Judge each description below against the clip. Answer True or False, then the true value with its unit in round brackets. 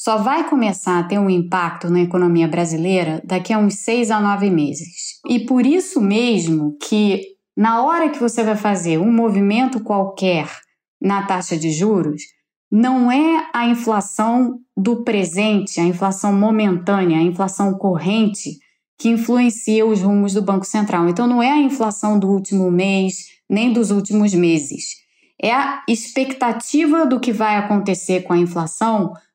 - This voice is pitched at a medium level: False (205 Hz)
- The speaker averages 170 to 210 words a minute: False (155 wpm)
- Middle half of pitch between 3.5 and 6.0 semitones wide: True (4.0 semitones)